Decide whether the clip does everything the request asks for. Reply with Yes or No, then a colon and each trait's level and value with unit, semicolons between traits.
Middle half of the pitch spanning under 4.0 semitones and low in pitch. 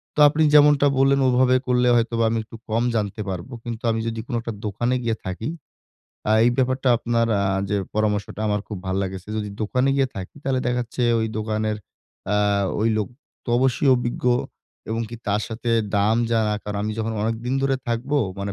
Yes: average, 2.9 semitones; low, 115 Hz